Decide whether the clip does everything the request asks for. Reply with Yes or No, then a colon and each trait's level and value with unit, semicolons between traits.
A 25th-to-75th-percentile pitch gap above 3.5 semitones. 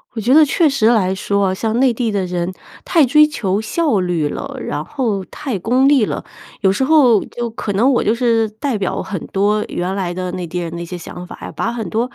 Yes: average, 5.0 semitones